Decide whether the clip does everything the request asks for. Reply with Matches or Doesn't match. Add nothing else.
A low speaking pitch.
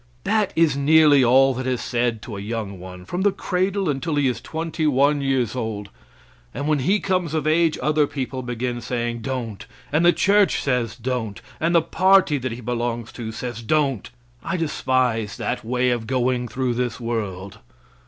Matches